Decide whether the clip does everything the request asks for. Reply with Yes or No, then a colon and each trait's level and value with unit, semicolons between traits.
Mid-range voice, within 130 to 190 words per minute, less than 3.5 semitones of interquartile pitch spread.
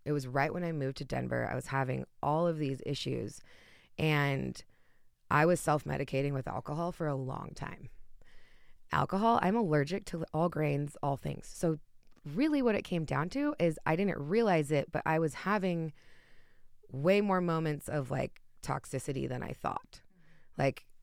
No: medium, 155 Hz; average, 170 wpm; average, 3.8 semitones